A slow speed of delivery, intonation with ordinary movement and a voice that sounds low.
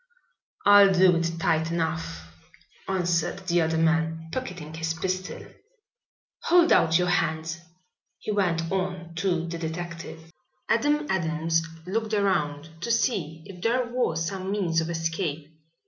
No: slow, 130 wpm; average, 3.0 semitones; medium, 170 Hz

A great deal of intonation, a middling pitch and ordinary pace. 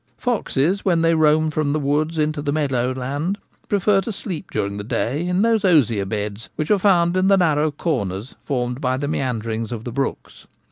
Yes: wide, 5.9 semitones; medium, 150 Hz; average, 195 wpm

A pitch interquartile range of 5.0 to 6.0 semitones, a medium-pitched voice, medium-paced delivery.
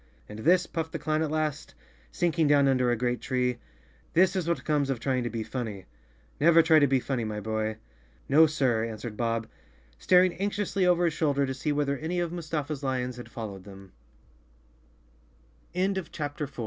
Yes: average, 5.3 semitones; medium, 145 Hz; average, 160 wpm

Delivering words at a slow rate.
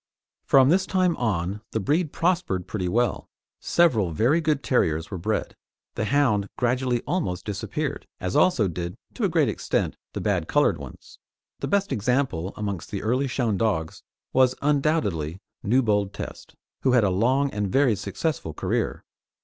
No: average, 155 wpm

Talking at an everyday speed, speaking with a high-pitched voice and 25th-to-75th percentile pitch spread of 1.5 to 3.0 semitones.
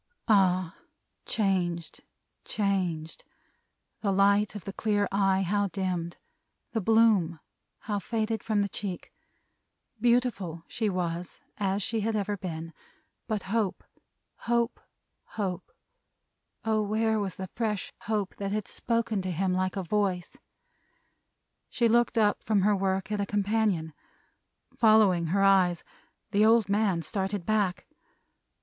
No: slow, 130 wpm; high, 200 Hz; average, 2.7 semitones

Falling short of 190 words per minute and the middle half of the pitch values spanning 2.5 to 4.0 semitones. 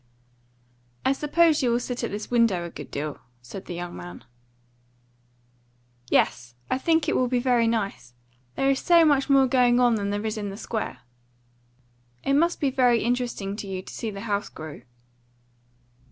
No: average, 175 wpm; average, 5.0 semitones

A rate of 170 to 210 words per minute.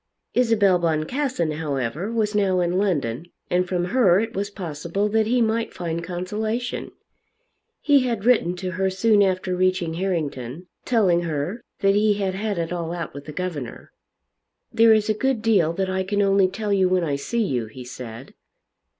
Yes: average, 175 wpm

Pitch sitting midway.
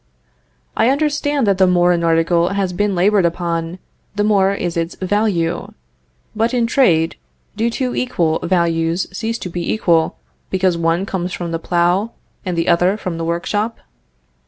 Yes: medium, 180 Hz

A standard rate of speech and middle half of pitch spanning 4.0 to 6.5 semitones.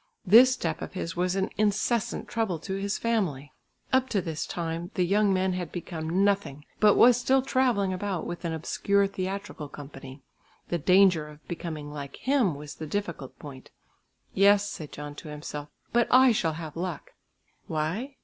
Yes: average, 170 wpm; average, 4.7 semitones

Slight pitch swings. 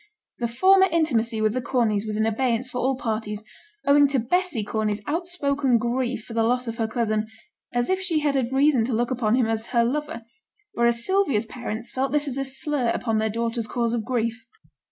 No: average, 3.4 semitones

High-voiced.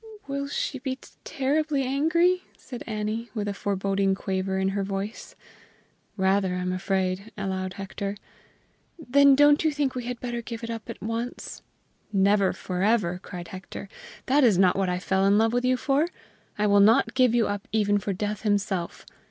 Yes: high, 210 Hz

